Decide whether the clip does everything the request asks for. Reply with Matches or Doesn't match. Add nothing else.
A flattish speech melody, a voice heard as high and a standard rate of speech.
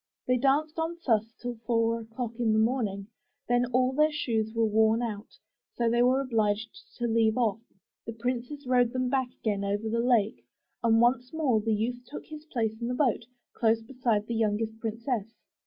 Matches